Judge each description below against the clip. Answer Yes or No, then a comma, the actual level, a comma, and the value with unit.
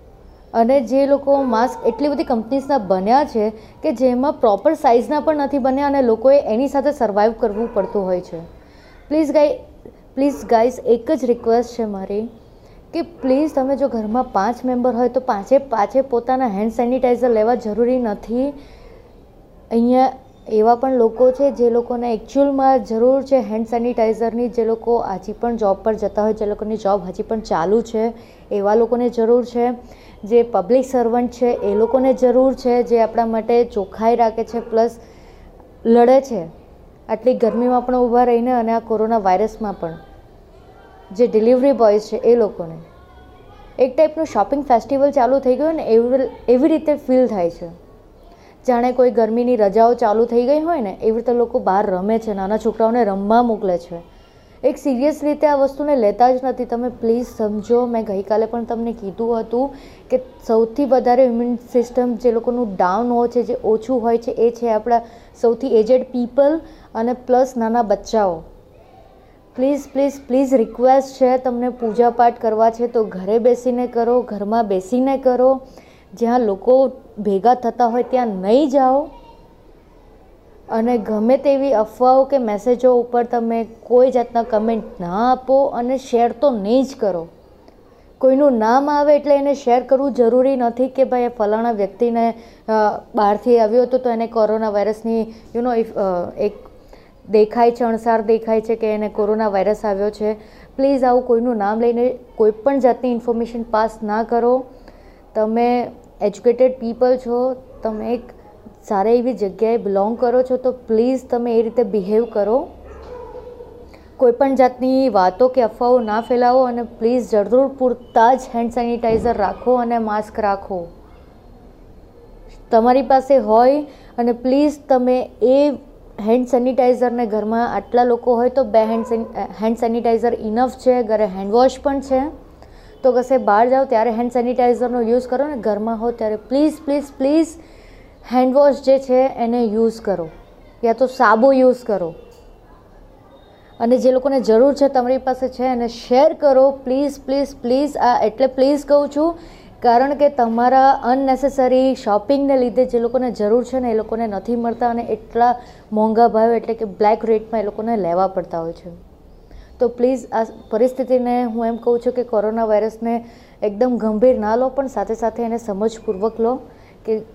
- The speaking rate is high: Yes, fast, 160 wpm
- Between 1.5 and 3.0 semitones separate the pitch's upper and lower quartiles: Yes, narrow, 2.5 semitones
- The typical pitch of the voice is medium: No, high, 240 Hz